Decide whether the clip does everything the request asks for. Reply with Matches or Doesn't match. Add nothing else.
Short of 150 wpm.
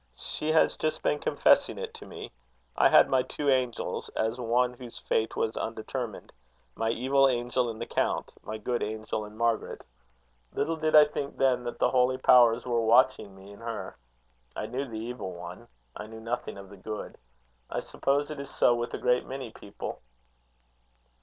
Doesn't match